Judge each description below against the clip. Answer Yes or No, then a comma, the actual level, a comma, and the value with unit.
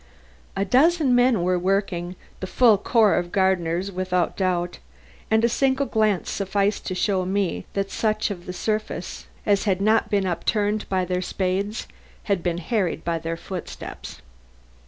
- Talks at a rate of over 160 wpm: No, average, 155 wpm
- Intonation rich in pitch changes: No, average, 2.9 semitones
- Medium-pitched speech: No, high, 195 Hz